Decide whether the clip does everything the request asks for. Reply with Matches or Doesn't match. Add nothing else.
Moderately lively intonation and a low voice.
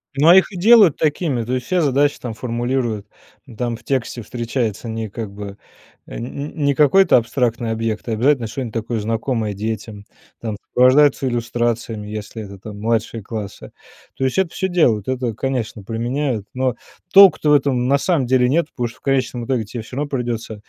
Matches